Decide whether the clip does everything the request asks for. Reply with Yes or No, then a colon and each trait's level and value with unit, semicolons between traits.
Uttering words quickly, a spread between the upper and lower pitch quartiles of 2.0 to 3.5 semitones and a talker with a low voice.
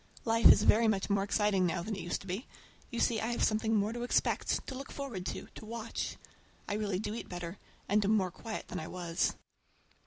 No: fast, 225 wpm; average, 3.2 semitones; high, 210 Hz